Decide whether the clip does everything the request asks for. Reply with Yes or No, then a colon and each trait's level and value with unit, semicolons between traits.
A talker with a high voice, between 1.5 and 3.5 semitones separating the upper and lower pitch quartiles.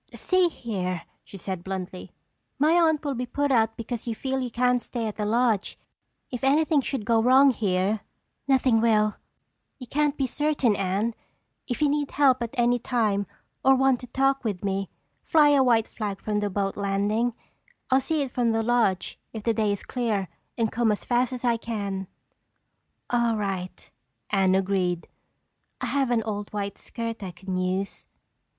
No: high, 230 Hz; average, 4.3 semitones